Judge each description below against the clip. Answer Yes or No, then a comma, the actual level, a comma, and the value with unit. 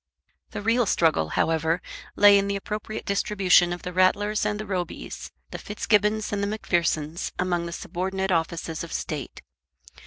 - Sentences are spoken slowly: No, average, 155 wpm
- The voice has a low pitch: No, high, 190 Hz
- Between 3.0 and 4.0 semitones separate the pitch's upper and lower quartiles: Yes, average, 3.4 semitones